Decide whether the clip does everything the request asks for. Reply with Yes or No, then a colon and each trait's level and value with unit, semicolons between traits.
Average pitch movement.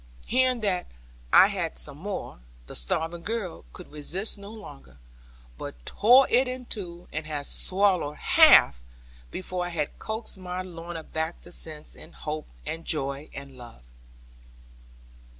Yes: average, 5.0 semitones